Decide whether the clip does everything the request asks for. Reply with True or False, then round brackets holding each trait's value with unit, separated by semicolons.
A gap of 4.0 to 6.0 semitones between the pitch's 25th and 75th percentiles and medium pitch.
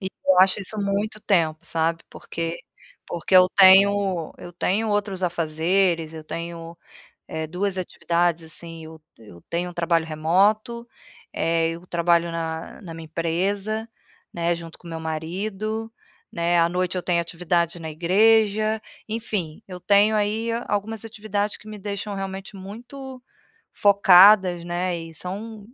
False (3.5 semitones; 180 Hz)